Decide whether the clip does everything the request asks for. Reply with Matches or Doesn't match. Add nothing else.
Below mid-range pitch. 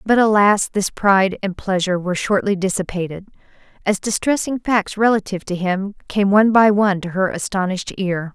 Doesn't match